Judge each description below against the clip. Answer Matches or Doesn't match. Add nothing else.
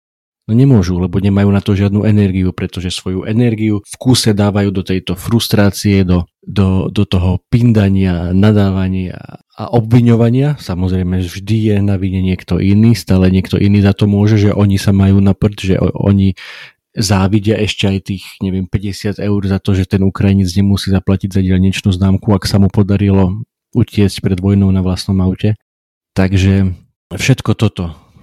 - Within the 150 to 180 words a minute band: Matches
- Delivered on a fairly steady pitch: Matches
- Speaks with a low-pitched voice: Matches